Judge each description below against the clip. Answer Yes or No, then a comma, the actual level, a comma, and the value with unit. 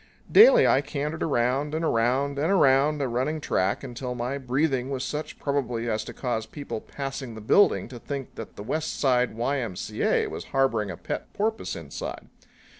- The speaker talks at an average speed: Yes, average, 175 wpm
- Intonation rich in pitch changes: No, average, 3.6 semitones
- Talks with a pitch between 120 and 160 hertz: Yes, low, 135 Hz